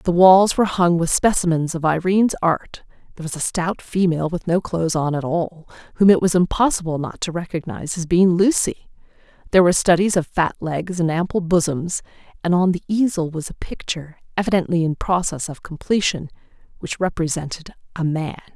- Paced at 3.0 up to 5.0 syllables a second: No, 5.6 syllables/s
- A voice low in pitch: No, medium, 170 Hz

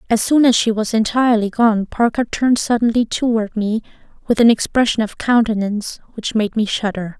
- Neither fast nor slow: Yes, average, 175 wpm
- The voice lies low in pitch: No, high, 225 Hz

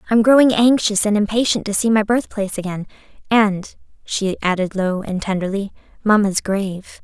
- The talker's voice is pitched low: No, high, 205 Hz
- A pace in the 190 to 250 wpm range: No, average, 155 wpm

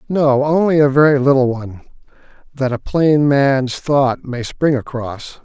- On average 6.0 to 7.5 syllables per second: No, 4.2 syllables/s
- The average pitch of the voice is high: No, low, 135 Hz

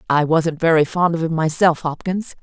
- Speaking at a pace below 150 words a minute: No, average, 200 wpm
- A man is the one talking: No, female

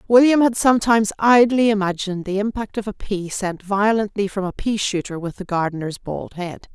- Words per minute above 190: No, average, 185 wpm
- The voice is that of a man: No, female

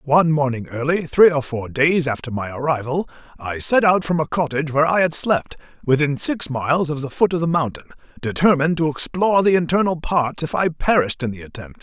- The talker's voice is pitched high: No, medium, 150 Hz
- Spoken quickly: Yes, fast, 210 wpm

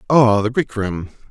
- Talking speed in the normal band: Yes, average, 185 wpm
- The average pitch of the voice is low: Yes, low, 115 Hz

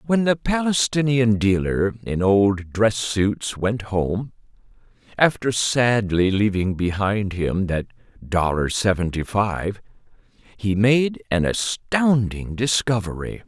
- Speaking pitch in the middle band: No, low, 105 Hz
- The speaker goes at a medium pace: No, slow, 100 wpm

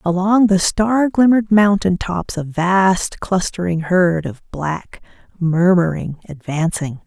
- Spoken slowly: Yes, slow, 120 wpm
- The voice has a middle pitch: Yes, medium, 180 Hz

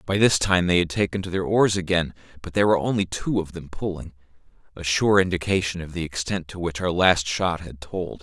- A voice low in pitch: Yes, very low, 90 Hz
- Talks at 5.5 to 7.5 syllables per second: Yes, 5.7 syllables/s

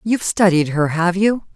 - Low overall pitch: No, medium, 185 Hz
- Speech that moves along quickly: No, average, 195 wpm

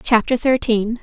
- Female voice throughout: Yes, female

